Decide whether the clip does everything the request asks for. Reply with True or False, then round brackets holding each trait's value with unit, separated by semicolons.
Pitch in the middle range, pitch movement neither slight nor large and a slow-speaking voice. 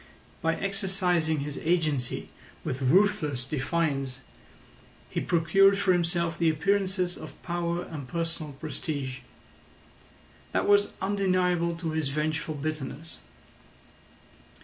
True (165 Hz; 3.1 semitones; 105 wpm)